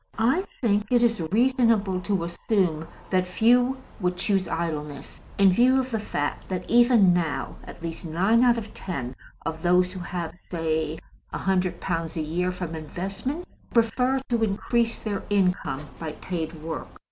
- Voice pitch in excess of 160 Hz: Yes, medium, 185 Hz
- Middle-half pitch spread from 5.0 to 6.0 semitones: Yes, wide, 5.5 semitones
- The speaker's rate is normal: Yes, average, 160 wpm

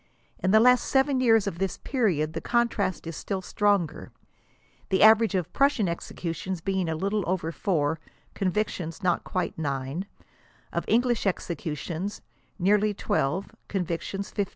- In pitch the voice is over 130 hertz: Yes, high, 190 Hz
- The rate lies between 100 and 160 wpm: Yes, average, 140 wpm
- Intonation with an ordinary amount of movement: Yes, average, 4.1 semitones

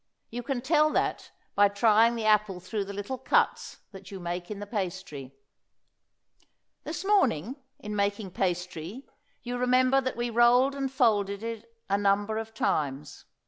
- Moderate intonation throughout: Yes, average, 3.8 semitones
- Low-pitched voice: No, high, 215 Hz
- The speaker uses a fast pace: No, average, 155 wpm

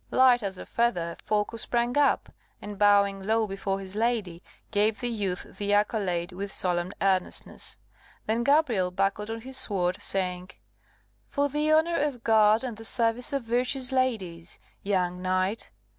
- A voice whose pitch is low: No, high, 210 Hz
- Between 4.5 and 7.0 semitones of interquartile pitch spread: No, average, 4.1 semitones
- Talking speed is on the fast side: No, average, 155 wpm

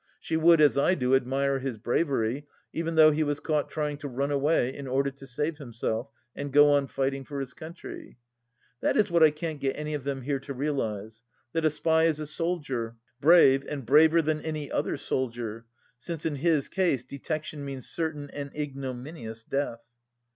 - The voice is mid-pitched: Yes, medium, 145 Hz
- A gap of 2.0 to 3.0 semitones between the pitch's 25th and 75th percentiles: Yes, average, 2.7 semitones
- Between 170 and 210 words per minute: Yes, average, 190 wpm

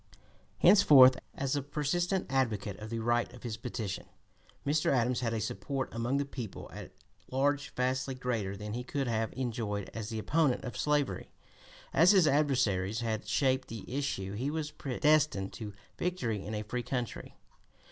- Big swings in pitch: No, average, 4.2 semitones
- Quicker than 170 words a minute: No, average, 160 wpm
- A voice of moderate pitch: No, low, 125 Hz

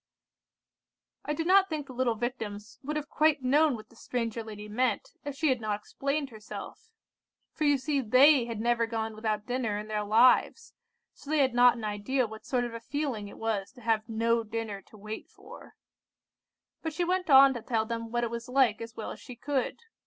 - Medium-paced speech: No, fast, 210 wpm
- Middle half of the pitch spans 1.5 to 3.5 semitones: No, average, 4.1 semitones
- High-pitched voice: Yes, high, 240 Hz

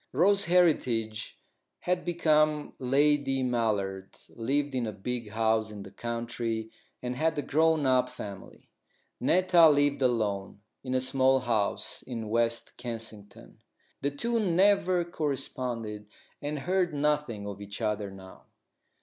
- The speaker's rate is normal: No, slow, 130 wpm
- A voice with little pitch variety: No, average, 5.3 semitones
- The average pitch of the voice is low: Yes, low, 125 Hz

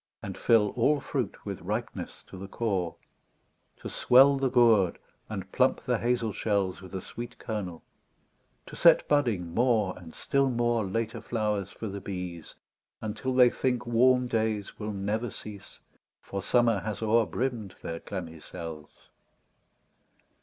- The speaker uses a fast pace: No, average, 145 wpm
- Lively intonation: No, average, 3.9 semitones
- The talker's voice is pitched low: Yes, low, 110 Hz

